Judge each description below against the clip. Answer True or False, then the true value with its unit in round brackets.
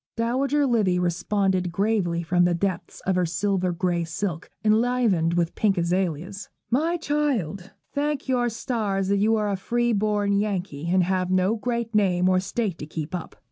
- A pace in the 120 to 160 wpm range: False (170 wpm)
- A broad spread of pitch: False (4.2 semitones)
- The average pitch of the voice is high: True (195 Hz)